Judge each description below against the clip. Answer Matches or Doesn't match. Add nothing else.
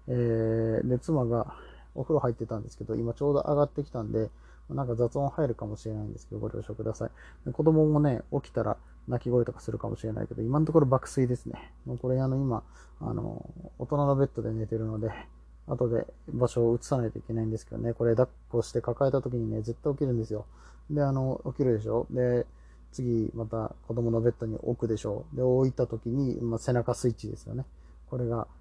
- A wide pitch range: Doesn't match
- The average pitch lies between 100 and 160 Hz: Matches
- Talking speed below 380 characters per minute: Doesn't match